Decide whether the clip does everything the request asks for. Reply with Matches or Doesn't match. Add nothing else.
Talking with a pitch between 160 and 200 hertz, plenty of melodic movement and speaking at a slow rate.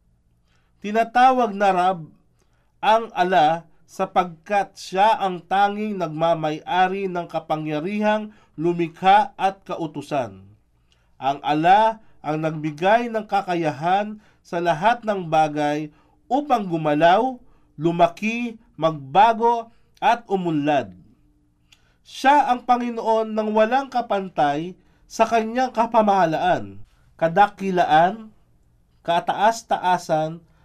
Matches